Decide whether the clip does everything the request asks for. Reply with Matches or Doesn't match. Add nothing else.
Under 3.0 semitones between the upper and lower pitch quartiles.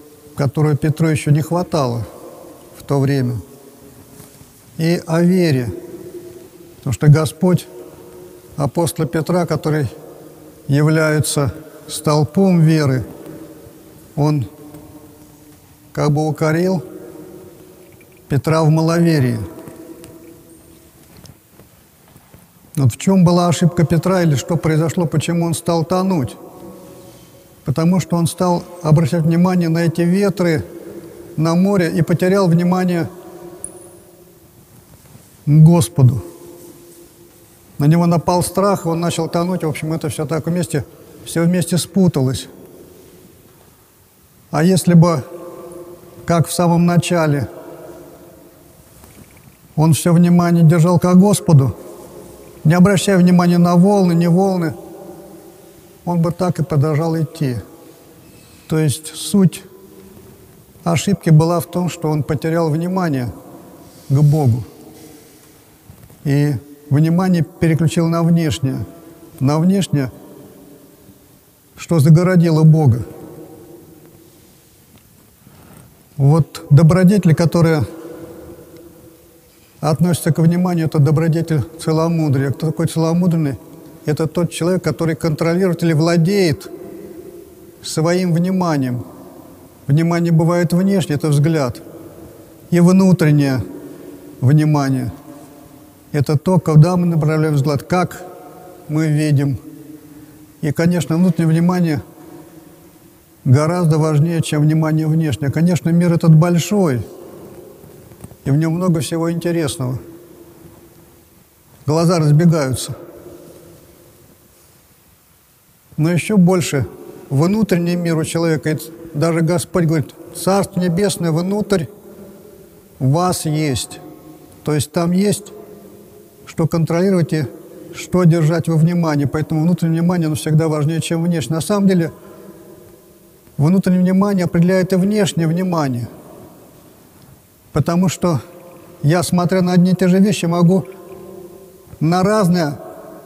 Matches